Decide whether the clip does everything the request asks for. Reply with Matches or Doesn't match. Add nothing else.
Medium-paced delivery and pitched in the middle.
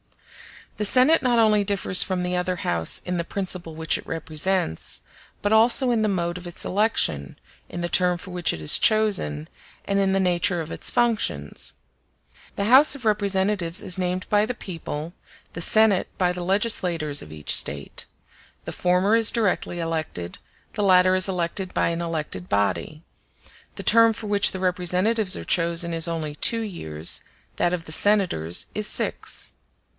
Matches